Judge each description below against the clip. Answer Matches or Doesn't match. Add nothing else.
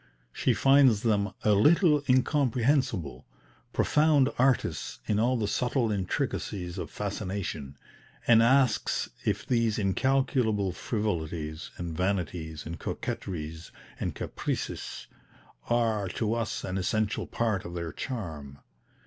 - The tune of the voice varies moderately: Doesn't match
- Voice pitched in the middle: Doesn't match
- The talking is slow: Matches